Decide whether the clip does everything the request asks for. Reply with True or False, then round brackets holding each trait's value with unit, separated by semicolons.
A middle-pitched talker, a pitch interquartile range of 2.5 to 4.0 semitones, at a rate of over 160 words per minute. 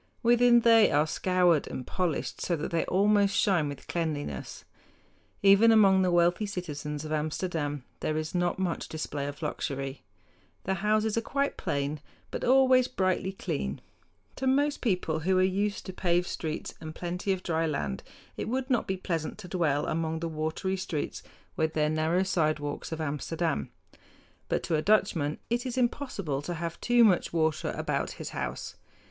False (175 Hz; 4.4 semitones; 170 wpm)